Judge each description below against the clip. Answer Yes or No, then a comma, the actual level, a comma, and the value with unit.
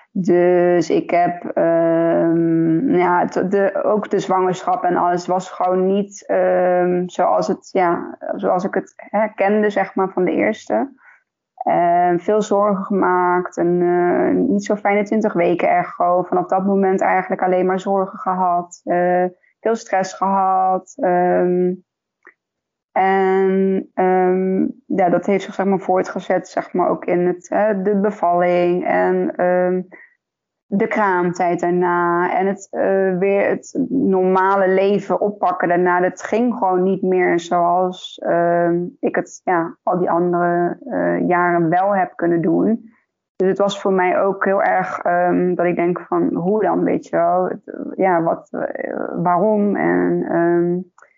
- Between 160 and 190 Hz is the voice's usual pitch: Yes, medium, 185 Hz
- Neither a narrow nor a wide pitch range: No, narrow, 1.9 semitones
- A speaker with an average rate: Yes, average, 150 wpm